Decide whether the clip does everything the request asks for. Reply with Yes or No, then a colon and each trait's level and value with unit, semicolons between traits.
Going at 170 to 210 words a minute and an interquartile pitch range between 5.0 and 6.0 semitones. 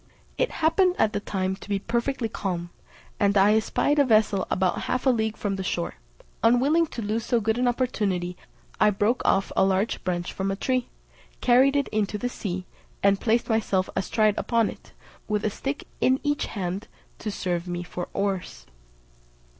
No: average, 180 wpm; average, 4.1 semitones